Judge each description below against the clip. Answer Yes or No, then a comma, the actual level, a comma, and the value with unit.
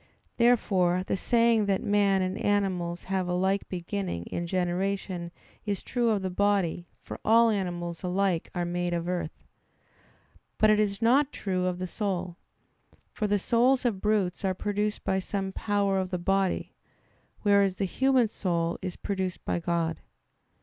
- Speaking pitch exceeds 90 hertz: Yes, high, 190 Hz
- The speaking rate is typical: Yes, average, 160 wpm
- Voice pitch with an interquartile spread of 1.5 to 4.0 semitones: Yes, narrow, 2.5 semitones